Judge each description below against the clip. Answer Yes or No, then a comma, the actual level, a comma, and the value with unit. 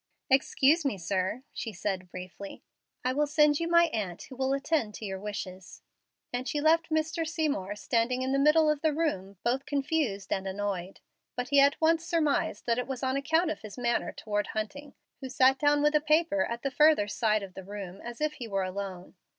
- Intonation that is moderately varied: No, wide, 6.7 semitones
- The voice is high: Yes, very high, 260 Hz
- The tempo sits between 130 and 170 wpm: No, fast, 205 wpm